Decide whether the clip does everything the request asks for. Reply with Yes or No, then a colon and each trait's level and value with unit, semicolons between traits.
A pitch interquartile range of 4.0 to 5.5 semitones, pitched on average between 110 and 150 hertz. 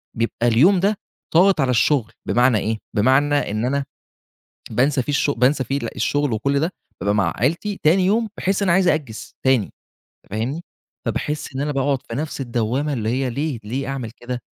Yes: average, 4.3 semitones; low, 135 Hz